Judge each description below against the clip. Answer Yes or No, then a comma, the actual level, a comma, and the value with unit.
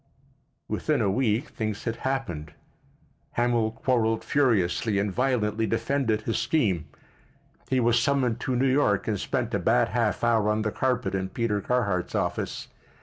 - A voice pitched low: Yes, low, 115 Hz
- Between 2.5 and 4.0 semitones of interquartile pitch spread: Yes, average, 3.4 semitones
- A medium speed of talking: Yes, average, 150 wpm